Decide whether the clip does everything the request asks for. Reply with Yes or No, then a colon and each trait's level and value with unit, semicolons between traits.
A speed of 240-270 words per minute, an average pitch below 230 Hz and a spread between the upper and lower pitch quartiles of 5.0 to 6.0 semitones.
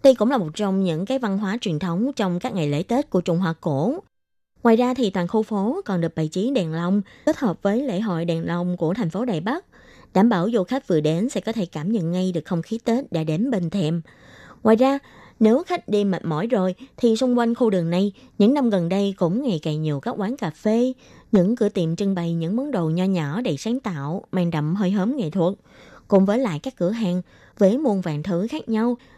Yes: fast, 250 wpm; high, 200 Hz; average, 5.3 semitones